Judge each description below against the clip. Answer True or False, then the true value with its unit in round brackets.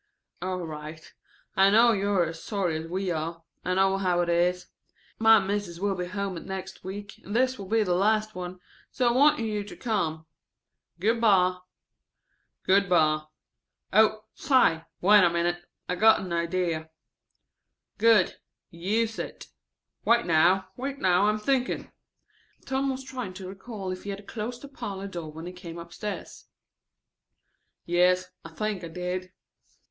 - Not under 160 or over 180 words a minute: True (165 wpm)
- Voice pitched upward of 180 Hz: True (190 Hz)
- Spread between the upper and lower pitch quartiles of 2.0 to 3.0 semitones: False (3.5 semitones)